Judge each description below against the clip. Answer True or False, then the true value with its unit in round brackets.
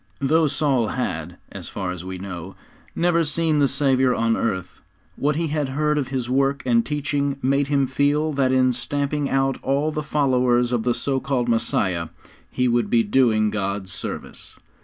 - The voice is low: True (130 Hz)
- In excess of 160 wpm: True (180 wpm)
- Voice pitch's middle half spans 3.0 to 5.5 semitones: True (3.7 semitones)